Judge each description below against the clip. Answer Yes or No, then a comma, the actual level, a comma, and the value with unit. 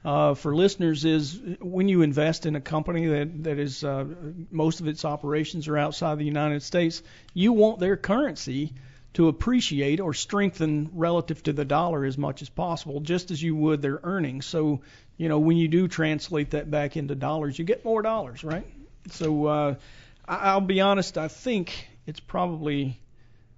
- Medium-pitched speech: Yes, medium, 155 Hz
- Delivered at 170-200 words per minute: Yes, average, 180 wpm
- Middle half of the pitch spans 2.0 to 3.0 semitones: Yes, average, 2.7 semitones